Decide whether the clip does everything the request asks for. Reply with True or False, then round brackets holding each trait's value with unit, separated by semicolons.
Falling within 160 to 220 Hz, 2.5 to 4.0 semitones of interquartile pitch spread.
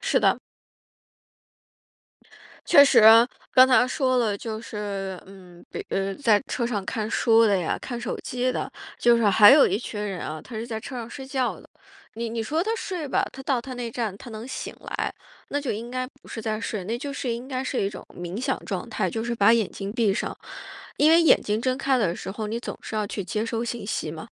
False (230 Hz; 3.6 semitones)